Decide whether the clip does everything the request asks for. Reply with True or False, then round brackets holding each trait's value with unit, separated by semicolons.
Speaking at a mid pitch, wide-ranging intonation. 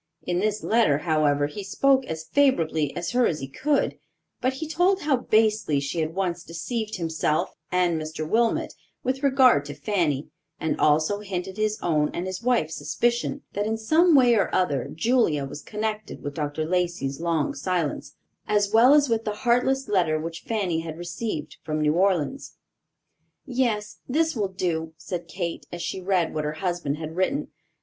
True (180 Hz; 6.5 semitones)